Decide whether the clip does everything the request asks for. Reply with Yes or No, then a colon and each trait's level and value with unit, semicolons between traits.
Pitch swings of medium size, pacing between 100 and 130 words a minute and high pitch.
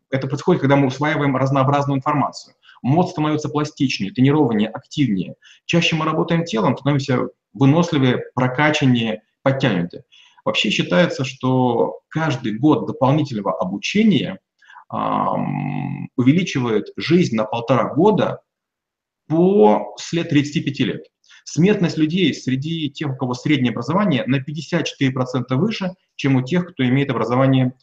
No: average, 3.6 semitones; average, 115 wpm; medium, 140 Hz